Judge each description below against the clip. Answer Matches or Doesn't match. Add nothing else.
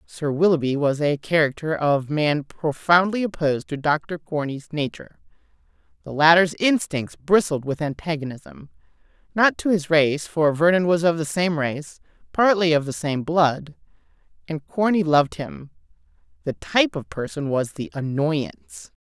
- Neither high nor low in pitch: Matches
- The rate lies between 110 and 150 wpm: Matches